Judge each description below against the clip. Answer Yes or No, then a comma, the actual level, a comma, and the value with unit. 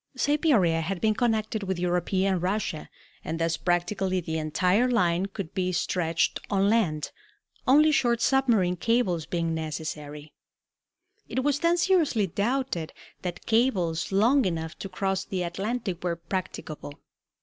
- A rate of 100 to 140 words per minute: Yes, slow, 135 wpm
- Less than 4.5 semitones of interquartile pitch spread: No, average, 5.3 semitones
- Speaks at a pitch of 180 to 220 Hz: Yes, high, 190 Hz